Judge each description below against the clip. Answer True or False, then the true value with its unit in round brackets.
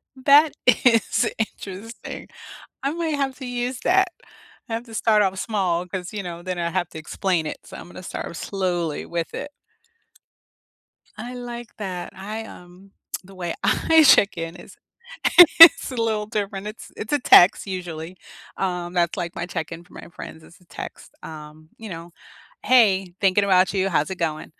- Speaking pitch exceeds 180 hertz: True (190 Hz)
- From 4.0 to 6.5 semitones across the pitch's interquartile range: True (4.7 semitones)